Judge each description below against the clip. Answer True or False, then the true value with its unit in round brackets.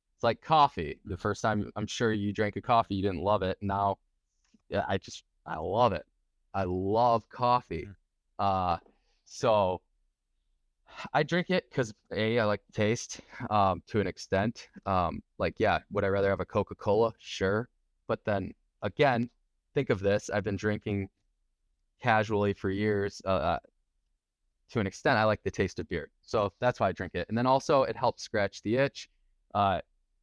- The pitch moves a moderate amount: True (3.1 semitones)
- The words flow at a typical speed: True (170 wpm)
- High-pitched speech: False (100 Hz)